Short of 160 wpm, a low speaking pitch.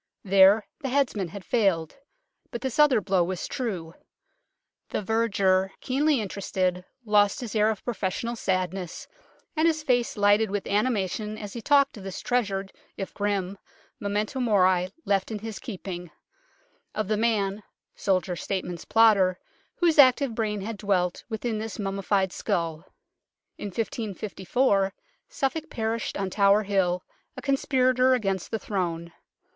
No: average, 140 wpm; high, 205 Hz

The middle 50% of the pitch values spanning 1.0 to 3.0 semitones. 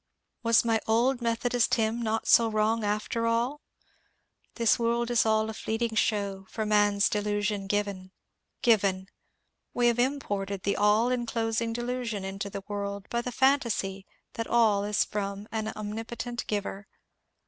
Yes: narrow, 2.5 semitones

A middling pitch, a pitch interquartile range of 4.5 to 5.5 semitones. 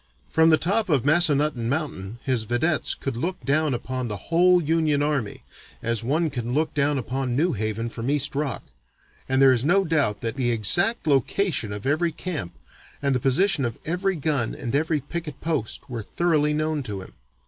Yes: medium, 145 Hz; average, 5.0 semitones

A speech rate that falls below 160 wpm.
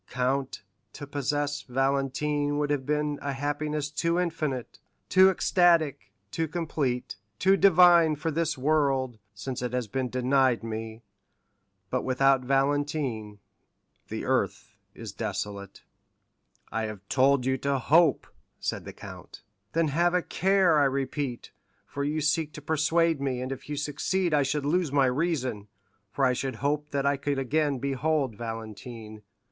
Yes: average, 150 wpm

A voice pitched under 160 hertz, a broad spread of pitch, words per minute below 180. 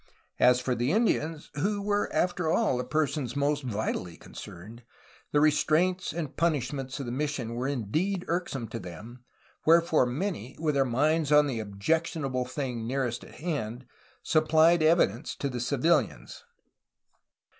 No: medium, 140 Hz; average, 4.6 semitones; average, 145 wpm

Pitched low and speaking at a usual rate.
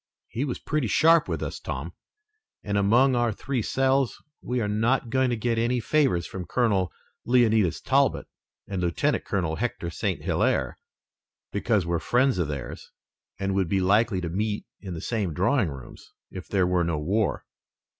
Yes: low, 105 Hz; average, 170 wpm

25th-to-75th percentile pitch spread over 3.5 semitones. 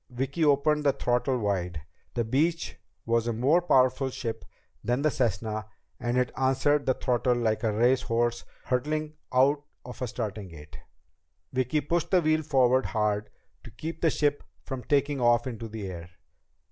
Yes: average, 3.9 semitones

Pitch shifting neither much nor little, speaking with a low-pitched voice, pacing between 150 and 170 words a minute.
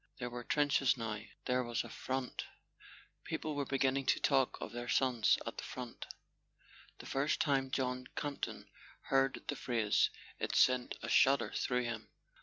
No: narrow, 1.8 semitones; low, 130 Hz; average, 155 wpm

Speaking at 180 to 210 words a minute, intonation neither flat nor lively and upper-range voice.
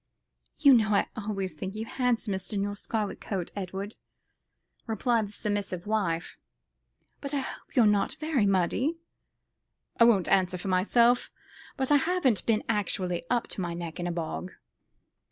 No: average, 155 wpm; average, 4.0 semitones; high, 205 Hz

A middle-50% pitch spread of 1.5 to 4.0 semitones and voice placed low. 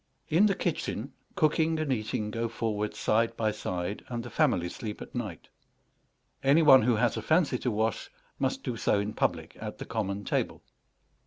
No: average, 5.0 semitones; low, 115 Hz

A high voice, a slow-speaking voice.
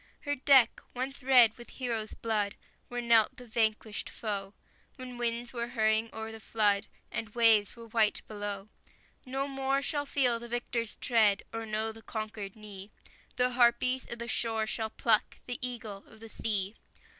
No: high, 225 Hz; average, 165 wpm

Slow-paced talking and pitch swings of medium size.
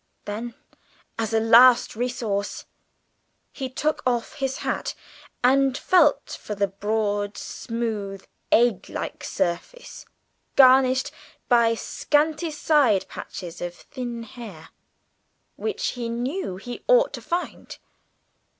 Yes: slow, 110 wpm; average, 4.5 semitones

